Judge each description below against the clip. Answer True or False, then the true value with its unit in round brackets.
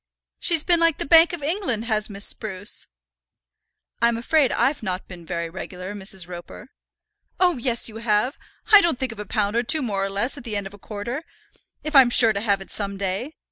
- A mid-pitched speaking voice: False (225 Hz)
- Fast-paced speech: True (215 wpm)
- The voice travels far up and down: True (5.7 semitones)